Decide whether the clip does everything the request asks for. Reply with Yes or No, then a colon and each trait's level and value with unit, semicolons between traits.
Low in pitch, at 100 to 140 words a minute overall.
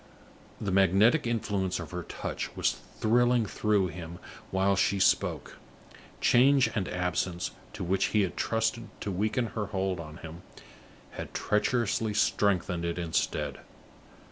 Yes: very low, 95 Hz; slow, 135 wpm